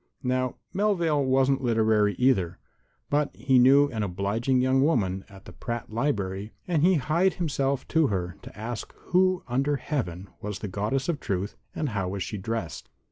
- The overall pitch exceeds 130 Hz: No, low, 125 Hz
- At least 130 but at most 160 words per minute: No, average, 170 wpm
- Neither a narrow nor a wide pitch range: No, wide, 6.0 semitones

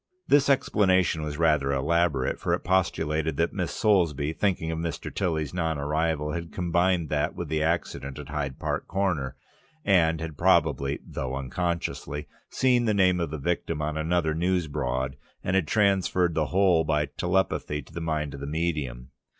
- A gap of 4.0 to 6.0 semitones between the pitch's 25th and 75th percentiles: No, average, 3.2 semitones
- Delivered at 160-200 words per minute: Yes, average, 170 wpm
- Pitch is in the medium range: No, very low, 80 Hz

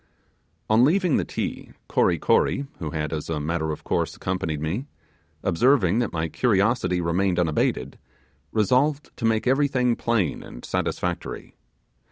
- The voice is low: Yes, very low, 95 Hz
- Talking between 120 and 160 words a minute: Yes, average, 140 wpm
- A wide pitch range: Yes, wide, 7.3 semitones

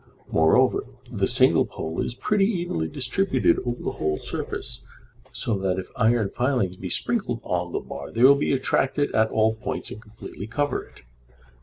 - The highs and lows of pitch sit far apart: Yes, wide, 6.5 semitones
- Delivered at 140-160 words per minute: No, average, 170 wpm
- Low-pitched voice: Yes, low, 110 Hz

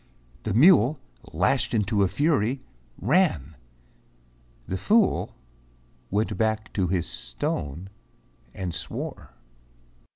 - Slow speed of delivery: Yes, slow, 95 wpm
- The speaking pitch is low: Yes, low, 105 Hz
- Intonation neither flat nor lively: No, wide, 6.1 semitones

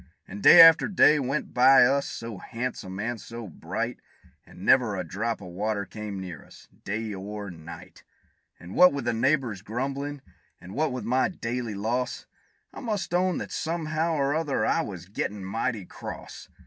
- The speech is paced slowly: No, average, 175 wpm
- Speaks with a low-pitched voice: Yes, low, 115 Hz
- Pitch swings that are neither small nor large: No, wide, 5.7 semitones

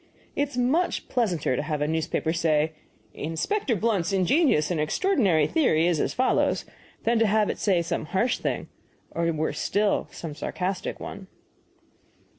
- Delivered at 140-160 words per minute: Yes, average, 155 wpm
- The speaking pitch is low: No, medium, 180 Hz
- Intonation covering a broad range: Yes, wide, 6.7 semitones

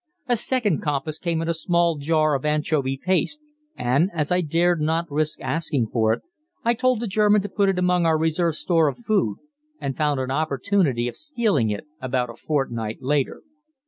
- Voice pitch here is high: No, medium, 160 Hz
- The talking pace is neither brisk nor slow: Yes, average, 190 wpm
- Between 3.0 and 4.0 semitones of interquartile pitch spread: No, average, 4.7 semitones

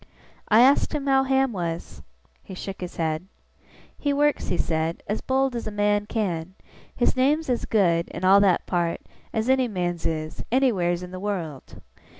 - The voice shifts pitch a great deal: Yes, wide, 6.8 semitones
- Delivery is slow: No, average, 175 wpm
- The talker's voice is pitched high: Yes, high, 200 Hz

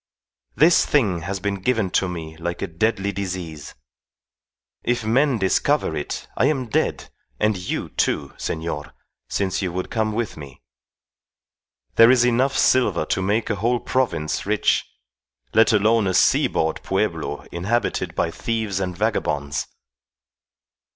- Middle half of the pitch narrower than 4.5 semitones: No, average, 5.0 semitones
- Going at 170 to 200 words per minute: No, slow, 135 wpm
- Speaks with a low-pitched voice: Yes, low, 100 Hz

